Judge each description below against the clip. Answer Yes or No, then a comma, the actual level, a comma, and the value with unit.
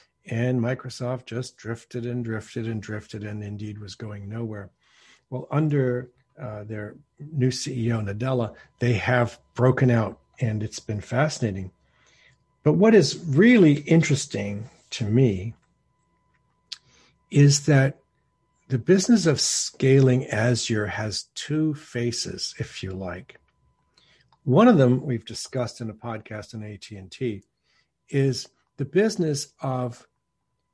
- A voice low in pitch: Yes, low, 120 Hz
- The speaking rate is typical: No, slow, 120 wpm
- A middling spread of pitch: Yes, average, 4.0 semitones